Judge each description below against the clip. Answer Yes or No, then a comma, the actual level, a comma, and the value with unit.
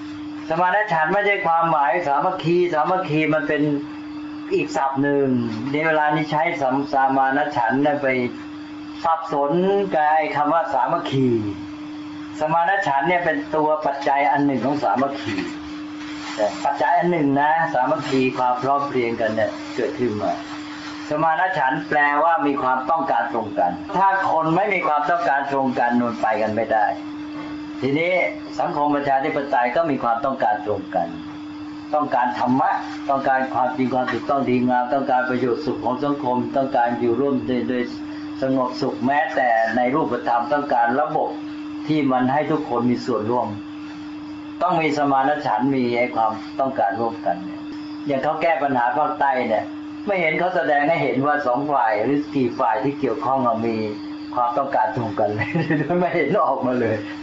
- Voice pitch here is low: No, medium, 150 Hz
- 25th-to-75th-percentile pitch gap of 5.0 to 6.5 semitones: Yes, average, 5.3 semitones